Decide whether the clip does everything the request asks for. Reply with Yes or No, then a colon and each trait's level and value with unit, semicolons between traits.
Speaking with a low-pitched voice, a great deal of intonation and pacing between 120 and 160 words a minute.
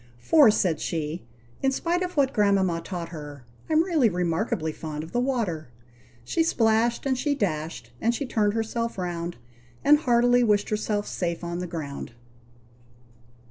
No: high, 205 Hz; wide, 6.6 semitones; average, 155 wpm